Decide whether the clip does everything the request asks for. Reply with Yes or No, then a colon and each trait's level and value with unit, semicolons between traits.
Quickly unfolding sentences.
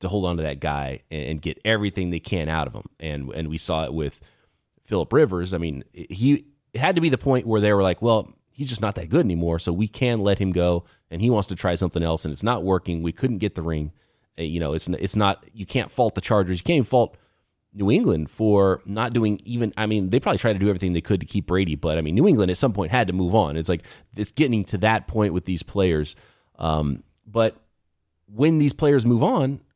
Yes: fast, 255 wpm